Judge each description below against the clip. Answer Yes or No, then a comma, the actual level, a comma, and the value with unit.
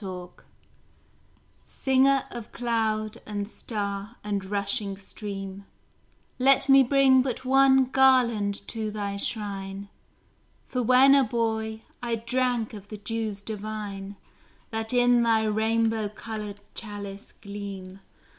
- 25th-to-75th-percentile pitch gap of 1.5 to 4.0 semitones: Yes, average, 3.2 semitones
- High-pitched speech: Yes, high, 220 Hz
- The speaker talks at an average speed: No, slow, 115 wpm